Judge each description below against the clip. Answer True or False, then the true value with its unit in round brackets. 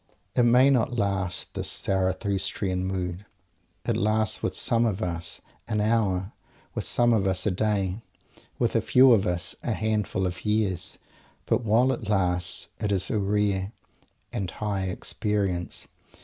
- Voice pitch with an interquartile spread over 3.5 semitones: False (2.8 semitones)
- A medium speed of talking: True (150 wpm)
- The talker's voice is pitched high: False (100 Hz)